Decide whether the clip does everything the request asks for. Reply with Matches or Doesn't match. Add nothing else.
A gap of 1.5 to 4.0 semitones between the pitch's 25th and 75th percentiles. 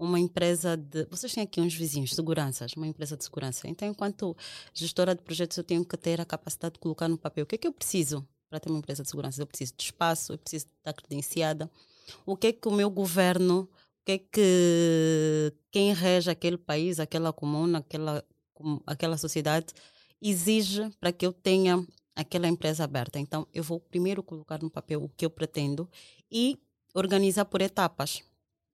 Matches